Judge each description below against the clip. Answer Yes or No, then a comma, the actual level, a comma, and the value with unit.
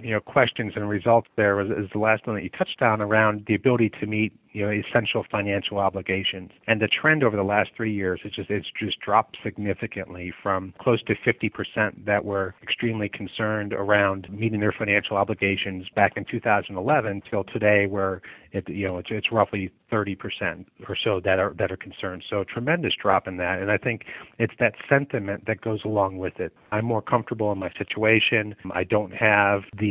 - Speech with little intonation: Yes, narrow, 1.9 semitones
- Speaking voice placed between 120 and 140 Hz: No, low, 105 Hz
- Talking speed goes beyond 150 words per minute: Yes, fast, 205 wpm